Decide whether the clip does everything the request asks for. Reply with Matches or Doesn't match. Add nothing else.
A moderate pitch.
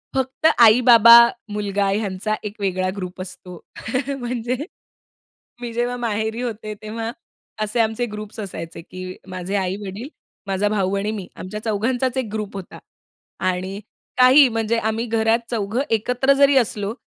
Doesn't match